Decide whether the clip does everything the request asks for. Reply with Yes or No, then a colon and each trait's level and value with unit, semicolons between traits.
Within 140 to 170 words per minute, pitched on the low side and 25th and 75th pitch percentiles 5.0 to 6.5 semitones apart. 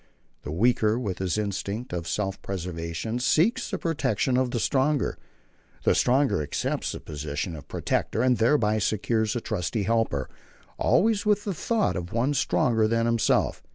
Yes: average, 155 wpm; low, 115 Hz; average, 5.3 semitones